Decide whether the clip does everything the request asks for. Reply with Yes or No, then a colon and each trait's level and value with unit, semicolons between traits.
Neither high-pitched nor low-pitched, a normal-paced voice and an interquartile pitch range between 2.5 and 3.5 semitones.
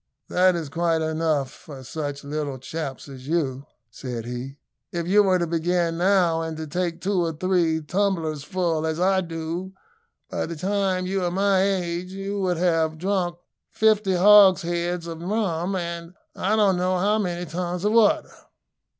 Yes: medium, 175 Hz; average, 165 wpm; average, 2.8 semitones